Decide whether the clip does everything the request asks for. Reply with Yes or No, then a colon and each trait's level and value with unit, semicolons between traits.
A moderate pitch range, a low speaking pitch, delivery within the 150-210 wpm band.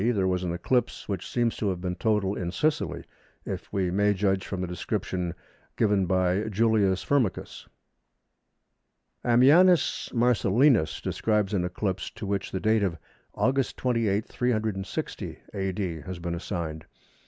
No: average, 3.5 semitones; low, 100 Hz; average, 140 wpm